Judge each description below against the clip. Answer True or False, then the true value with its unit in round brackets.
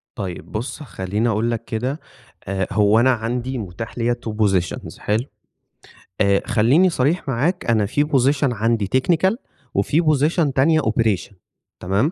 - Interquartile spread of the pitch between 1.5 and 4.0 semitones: False (5.0 semitones)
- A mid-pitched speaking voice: False (115 Hz)